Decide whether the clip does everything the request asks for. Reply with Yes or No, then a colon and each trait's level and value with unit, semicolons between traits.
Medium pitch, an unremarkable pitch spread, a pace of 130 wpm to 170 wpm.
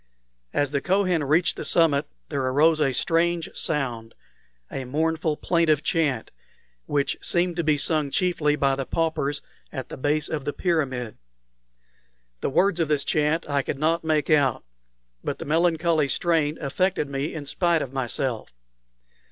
Yes: medium, 150 Hz; average, 3.0 semitones; average, 155 wpm